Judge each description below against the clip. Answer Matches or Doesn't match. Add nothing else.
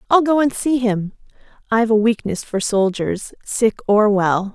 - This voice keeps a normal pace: Matches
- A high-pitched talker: Matches